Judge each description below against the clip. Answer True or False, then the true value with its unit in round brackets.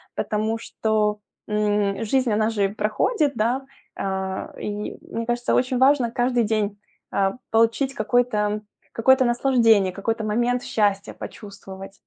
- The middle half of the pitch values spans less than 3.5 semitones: True (2.8 semitones)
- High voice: True (220 Hz)